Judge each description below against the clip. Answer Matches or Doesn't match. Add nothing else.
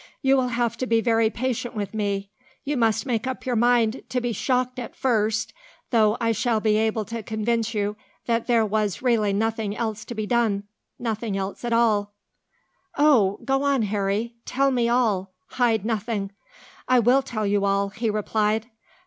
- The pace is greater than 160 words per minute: Matches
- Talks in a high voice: Matches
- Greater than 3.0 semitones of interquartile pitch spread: Doesn't match